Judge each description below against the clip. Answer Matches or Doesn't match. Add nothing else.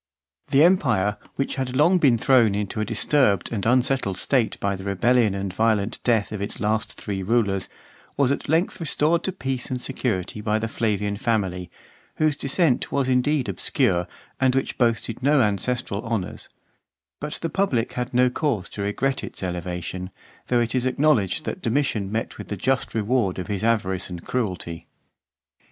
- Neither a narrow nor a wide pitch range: Matches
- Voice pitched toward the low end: Matches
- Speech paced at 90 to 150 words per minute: Doesn't match